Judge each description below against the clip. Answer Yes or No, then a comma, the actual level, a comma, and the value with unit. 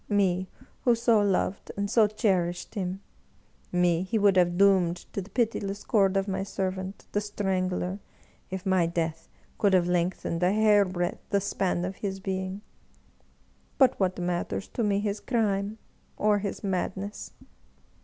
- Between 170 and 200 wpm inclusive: No, average, 155 wpm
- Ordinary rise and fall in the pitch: No, narrow, 2.0 semitones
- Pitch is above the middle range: Yes, high, 195 Hz